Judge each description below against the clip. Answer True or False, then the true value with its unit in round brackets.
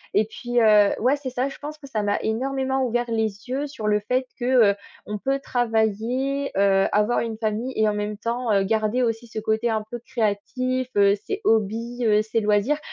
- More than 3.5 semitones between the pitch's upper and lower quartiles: False (3.2 semitones)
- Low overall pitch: False (225 Hz)